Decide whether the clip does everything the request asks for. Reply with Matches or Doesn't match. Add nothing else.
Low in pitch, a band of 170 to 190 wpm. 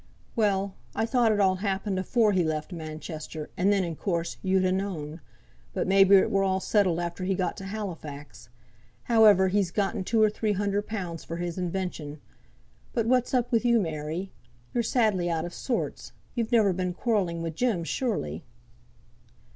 Doesn't match